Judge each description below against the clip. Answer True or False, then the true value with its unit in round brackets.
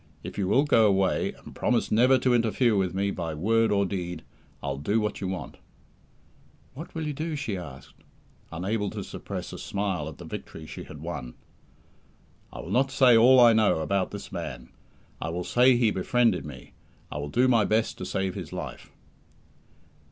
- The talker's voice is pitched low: True (100 Hz)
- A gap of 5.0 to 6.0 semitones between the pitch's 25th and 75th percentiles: True (5.5 semitones)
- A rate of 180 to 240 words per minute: True (190 wpm)